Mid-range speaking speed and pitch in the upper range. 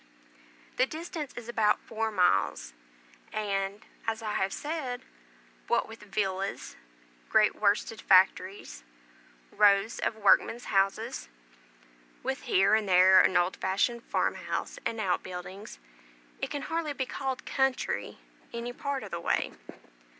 No: slow, 130 wpm; high, 215 Hz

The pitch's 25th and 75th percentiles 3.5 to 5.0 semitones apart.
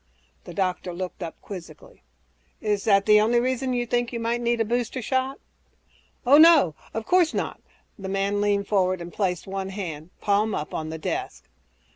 Yes: average, 4.3 semitones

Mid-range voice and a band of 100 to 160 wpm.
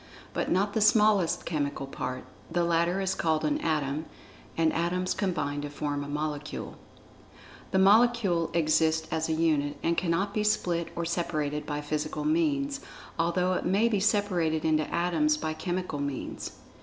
Yes: medium, 165 Hz; average, 155 wpm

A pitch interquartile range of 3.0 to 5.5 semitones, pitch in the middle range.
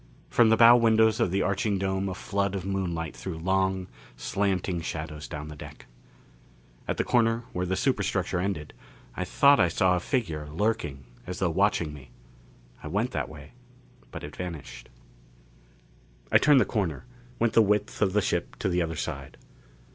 No: average, 4.1 semitones; very low, 95 Hz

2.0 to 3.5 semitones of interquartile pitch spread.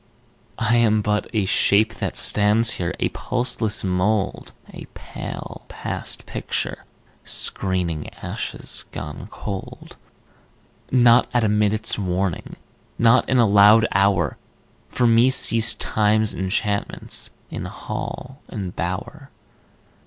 Yes: average, 2.8 semitones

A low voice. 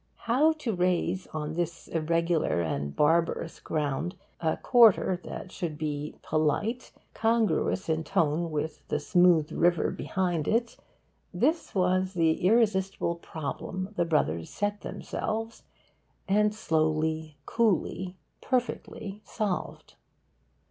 No: medium, 175 Hz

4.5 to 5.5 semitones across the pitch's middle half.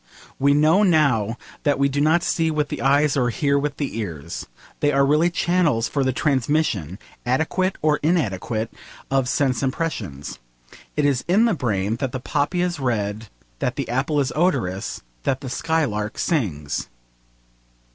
Yes: average, 5.2 semitones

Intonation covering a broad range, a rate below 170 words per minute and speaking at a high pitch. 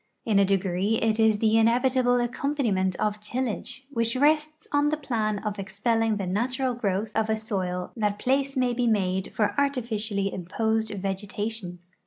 No: average, 3.7 semitones; average, 160 wpm; high, 220 Hz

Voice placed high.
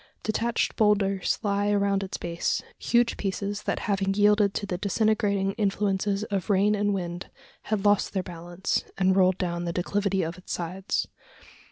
Yes: high, 195 Hz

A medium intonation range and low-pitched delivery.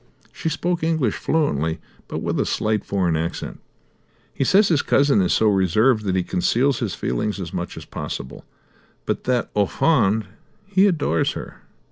No: wide, 8.2 semitones; low, 110 Hz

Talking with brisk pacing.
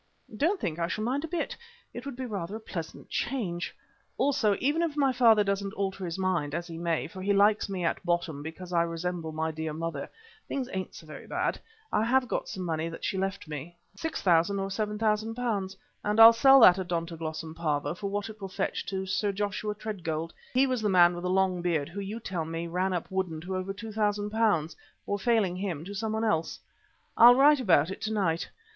Yes: fast, 210 wpm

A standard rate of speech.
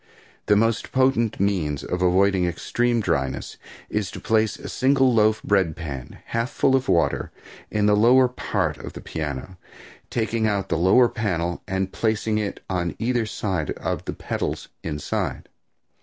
Yes: average, 155 wpm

